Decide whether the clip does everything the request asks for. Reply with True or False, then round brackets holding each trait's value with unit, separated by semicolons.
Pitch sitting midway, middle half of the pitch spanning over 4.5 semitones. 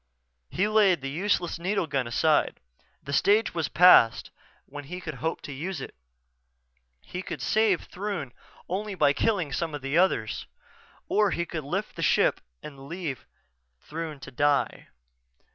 True (165 Hz; 5.0 semitones)